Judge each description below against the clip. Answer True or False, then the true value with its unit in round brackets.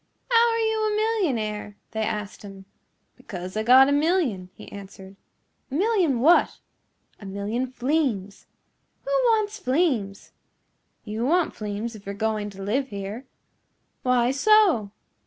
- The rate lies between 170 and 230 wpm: False (140 wpm)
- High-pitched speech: True (240 Hz)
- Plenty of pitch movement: True (8.9 semitones)